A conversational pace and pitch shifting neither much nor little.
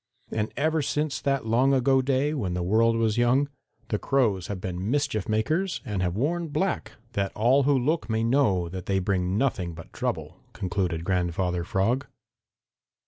No: average, 170 wpm; wide, 6.5 semitones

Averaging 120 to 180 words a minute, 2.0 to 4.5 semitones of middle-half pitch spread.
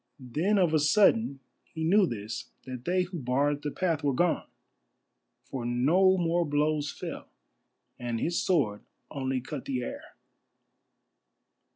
No: average, 140 wpm; average, 5.3 semitones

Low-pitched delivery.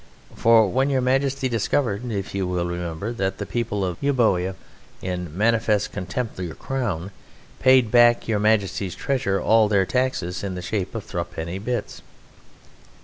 Yes: low, 105 Hz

